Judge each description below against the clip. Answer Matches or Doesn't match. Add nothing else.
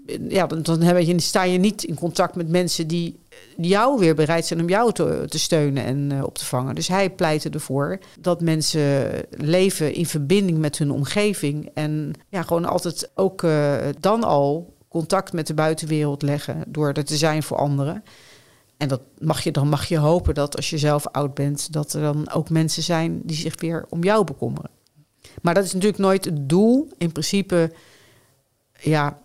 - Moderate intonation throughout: Matches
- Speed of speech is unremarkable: Matches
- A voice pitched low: Doesn't match